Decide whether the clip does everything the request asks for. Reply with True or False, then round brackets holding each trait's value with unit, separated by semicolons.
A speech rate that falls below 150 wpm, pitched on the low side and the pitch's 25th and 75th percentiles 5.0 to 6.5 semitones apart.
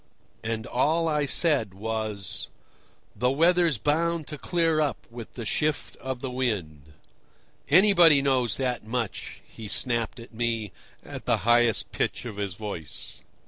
True (140 wpm; 125 Hz; 5.4 semitones)